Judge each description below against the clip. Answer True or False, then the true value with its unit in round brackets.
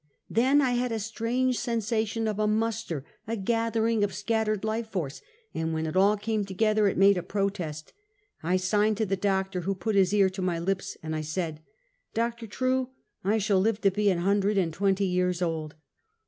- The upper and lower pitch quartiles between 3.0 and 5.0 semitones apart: True (3.3 semitones)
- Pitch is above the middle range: True (200 Hz)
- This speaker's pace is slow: False (200 wpm)